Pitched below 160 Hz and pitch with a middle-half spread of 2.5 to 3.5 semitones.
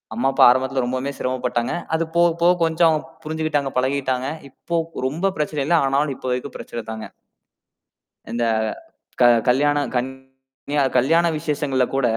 Yes: low, 135 Hz; average, 2.9 semitones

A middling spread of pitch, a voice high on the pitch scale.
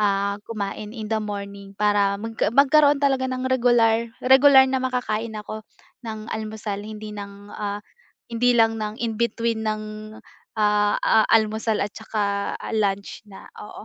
No: narrow, 2.1 semitones; high, 215 Hz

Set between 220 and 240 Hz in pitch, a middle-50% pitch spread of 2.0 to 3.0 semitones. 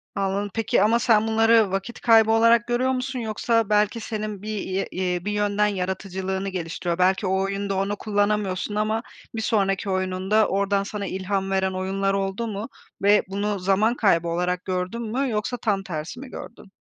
No: high, 200 Hz; narrow, 2.4 semitones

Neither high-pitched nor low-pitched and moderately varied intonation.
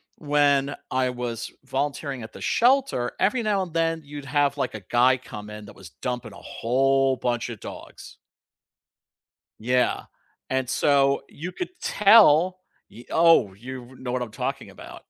No: low, 130 Hz; average, 3.5 semitones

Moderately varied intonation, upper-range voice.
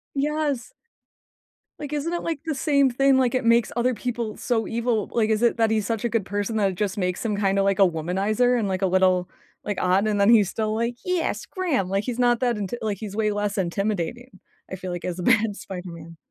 Yes: average, 3.9 semitones; high, 215 Hz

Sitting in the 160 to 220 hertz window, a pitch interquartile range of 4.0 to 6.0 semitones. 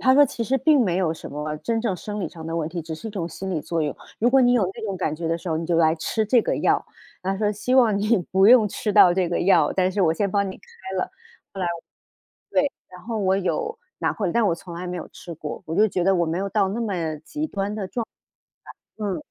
Yes: high, 190 Hz; average, 4.5 semitones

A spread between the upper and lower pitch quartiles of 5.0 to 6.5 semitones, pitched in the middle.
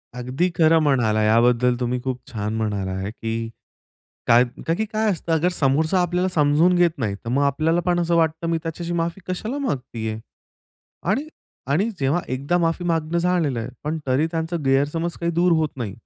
Yes: wide, 5.6 semitones; medium, 155 Hz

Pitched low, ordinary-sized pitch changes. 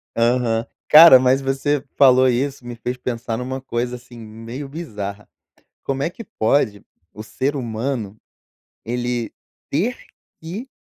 Yes: low, 125 Hz; average, 3.0 semitones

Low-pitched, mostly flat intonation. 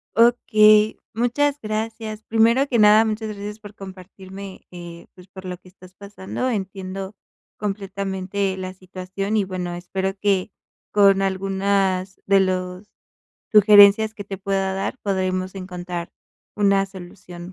No: high, 195 Hz; narrow, 2.1 semitones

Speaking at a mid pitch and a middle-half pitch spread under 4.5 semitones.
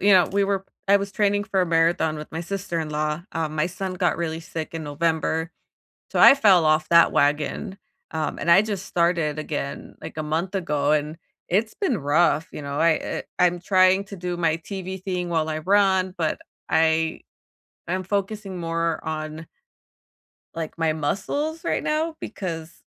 Yes: medium, 170 Hz; average, 3.3 semitones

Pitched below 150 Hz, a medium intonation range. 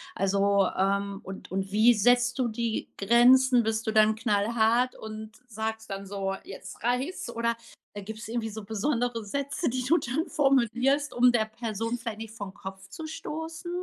No: high, 225 Hz; average, 3.2 semitones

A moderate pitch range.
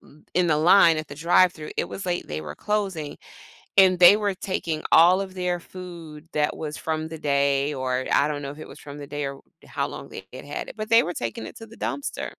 Yes: average, 4.1 semitones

